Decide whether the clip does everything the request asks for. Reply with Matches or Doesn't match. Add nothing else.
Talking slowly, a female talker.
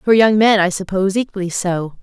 Doesn't match